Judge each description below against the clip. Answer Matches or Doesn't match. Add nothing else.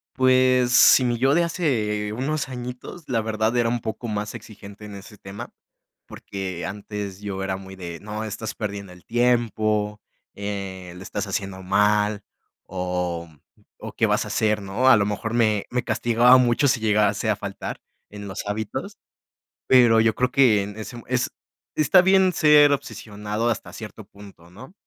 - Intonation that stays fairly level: Doesn't match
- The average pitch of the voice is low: Matches